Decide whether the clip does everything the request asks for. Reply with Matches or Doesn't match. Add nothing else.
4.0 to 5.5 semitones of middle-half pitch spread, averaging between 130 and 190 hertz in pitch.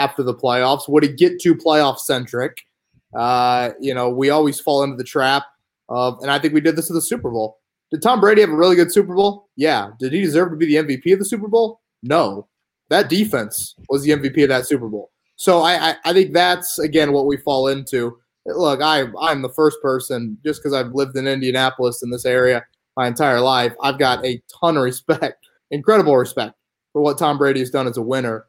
Matches